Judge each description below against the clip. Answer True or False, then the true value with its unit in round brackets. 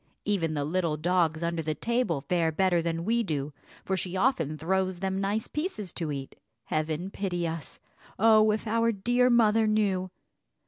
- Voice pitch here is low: False (185 Hz)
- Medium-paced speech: True (170 wpm)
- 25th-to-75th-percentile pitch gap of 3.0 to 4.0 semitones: False (4.8 semitones)